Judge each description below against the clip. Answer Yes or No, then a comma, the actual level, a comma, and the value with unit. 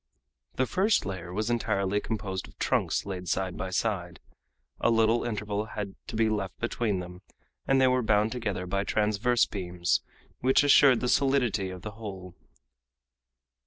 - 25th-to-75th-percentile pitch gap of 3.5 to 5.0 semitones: Yes, average, 3.9 semitones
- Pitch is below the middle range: Yes, low, 105 Hz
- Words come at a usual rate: Yes, average, 160 wpm